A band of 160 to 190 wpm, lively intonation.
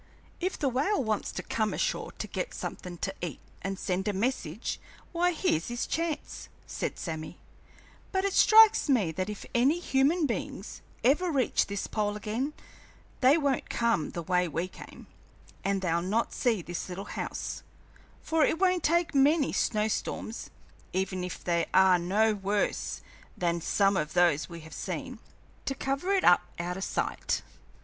Yes: average, 165 wpm; wide, 7.7 semitones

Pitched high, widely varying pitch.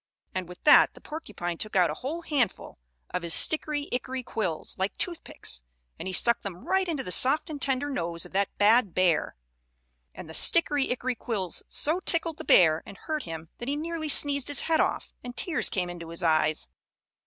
Yes: high, 240 Hz; wide, 8.8 semitones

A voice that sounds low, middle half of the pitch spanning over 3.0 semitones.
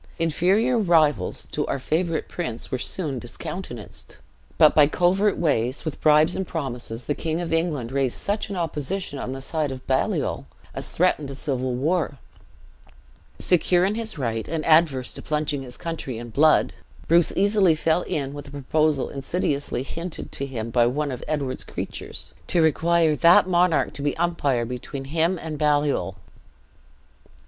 No: medium, 150 Hz; average, 4.2 semitones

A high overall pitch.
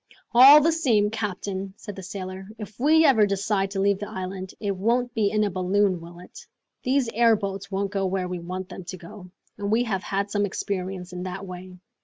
Yes: high, 195 Hz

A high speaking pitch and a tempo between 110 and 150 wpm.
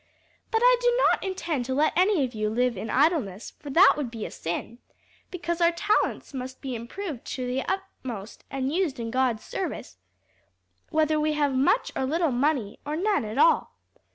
No: very high, 285 Hz; average, 185 wpm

